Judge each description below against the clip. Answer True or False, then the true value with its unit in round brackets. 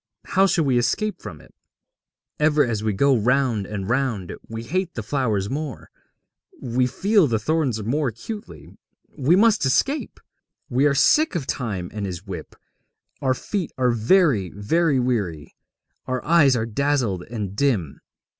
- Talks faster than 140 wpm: True (155 wpm)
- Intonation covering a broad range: True (5.8 semitones)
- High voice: False (130 Hz)